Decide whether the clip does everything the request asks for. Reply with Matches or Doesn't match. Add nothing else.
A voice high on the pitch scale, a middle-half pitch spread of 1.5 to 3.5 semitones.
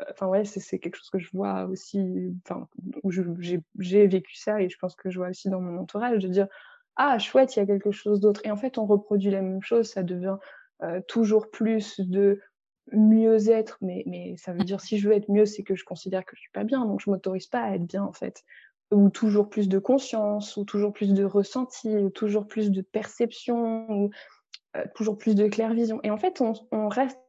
Matches